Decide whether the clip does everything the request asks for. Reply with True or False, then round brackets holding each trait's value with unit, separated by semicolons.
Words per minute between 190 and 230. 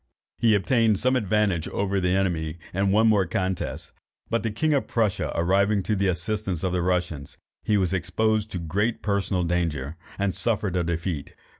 False (175 wpm)